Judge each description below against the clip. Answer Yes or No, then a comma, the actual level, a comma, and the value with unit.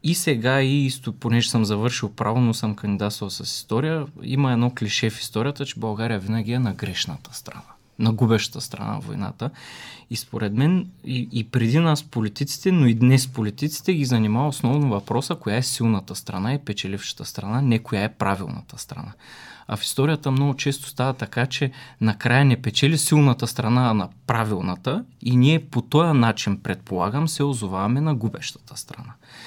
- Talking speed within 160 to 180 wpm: Yes, average, 175 wpm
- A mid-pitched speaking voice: No, low, 120 Hz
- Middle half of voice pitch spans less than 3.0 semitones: No, average, 4.2 semitones